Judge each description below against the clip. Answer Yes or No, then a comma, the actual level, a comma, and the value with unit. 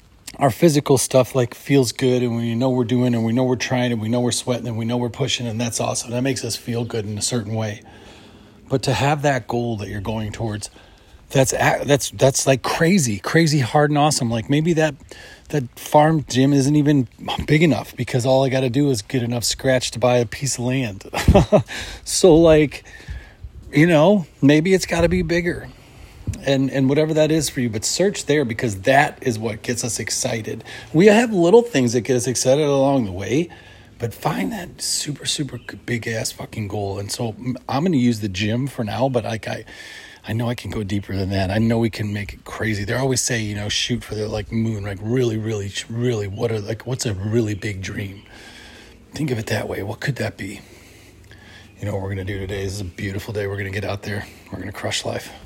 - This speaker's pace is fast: Yes, fast, 230 wpm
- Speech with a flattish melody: No, average, 4.0 semitones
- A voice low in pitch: Yes, low, 120 Hz